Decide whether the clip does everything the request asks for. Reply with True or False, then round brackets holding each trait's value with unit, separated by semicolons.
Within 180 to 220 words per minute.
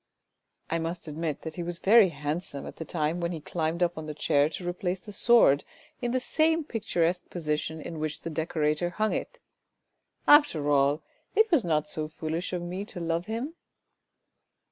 True (190 wpm)